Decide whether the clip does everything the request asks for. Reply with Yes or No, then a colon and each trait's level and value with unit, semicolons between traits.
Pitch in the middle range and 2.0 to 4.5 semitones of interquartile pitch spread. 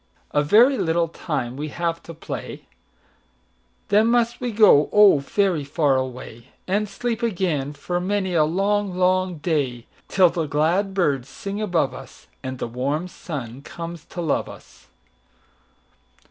No: medium, 170 Hz; average, 5.3 semitones